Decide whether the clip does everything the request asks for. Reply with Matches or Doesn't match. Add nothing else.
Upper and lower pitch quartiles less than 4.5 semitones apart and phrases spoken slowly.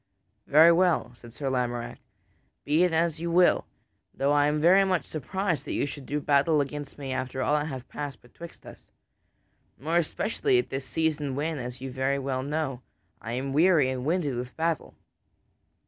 Doesn't match